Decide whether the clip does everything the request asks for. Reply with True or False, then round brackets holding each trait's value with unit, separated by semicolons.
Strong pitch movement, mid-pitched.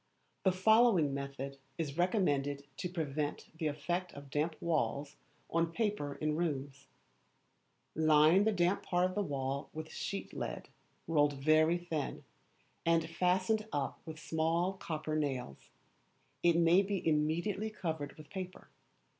False (3.8 semitones; 160 Hz)